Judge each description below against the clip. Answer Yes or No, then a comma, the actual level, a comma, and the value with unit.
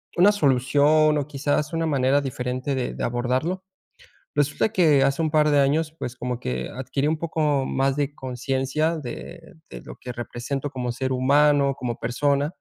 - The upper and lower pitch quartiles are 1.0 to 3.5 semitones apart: Yes, average, 2.9 semitones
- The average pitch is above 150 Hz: No, medium, 140 Hz